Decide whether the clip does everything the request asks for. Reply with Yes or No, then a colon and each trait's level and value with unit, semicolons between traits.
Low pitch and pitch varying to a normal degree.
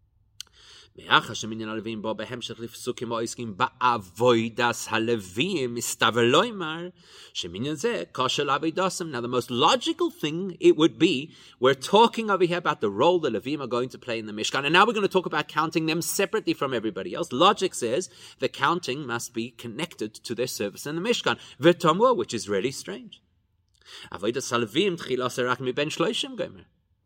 No: low, 125 Hz; wide, 6.6 semitones